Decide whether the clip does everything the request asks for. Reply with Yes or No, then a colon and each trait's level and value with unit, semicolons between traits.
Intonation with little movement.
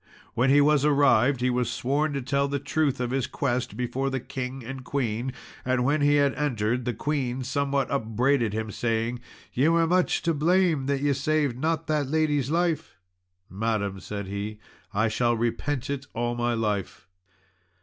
No: average, 3.3 semitones